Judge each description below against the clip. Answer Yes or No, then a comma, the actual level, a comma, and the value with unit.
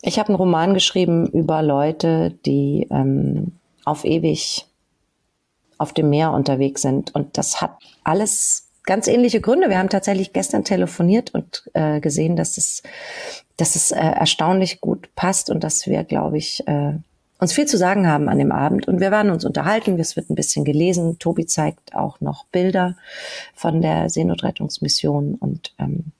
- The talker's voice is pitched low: No, medium, 170 Hz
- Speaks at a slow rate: No, average, 165 wpm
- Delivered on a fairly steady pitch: No, average, 4.0 semitones